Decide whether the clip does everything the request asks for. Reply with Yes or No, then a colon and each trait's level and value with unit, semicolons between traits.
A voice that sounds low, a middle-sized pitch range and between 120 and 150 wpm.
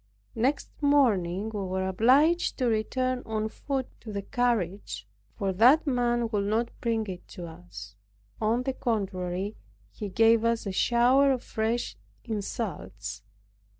No: high, 220 Hz; average, 4.4 semitones; average, 140 wpm